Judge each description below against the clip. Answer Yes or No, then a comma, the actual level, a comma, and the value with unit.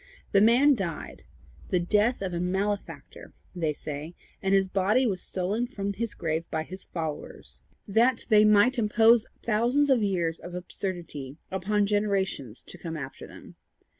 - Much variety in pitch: No, average, 3.8 semitones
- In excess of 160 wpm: No, average, 155 wpm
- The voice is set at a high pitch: Yes, high, 195 Hz